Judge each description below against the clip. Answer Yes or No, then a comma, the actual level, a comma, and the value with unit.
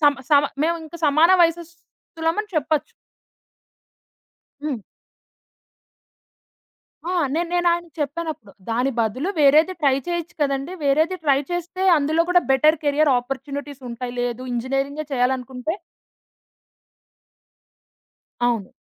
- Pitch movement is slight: No, average, 4.0 semitones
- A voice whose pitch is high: Yes, very high, 295 Hz